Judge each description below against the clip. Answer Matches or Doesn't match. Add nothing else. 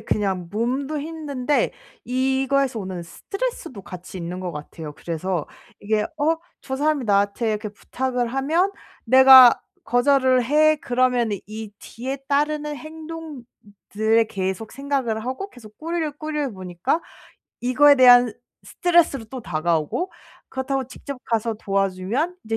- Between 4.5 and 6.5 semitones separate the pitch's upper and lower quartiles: Matches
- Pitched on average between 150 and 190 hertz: Doesn't match